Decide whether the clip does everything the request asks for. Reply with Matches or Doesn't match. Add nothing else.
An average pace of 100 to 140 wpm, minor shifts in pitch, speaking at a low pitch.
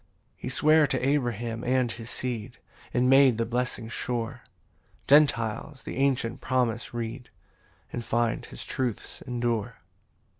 Matches